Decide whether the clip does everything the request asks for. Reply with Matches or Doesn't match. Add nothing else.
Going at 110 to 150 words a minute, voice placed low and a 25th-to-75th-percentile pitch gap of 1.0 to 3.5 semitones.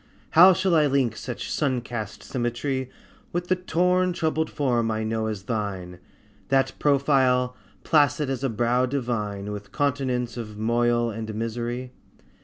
Doesn't match